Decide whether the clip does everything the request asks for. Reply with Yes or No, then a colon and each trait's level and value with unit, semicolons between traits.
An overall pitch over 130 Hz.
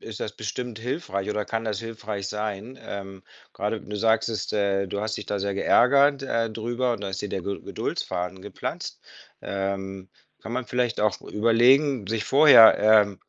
No: low, 105 Hz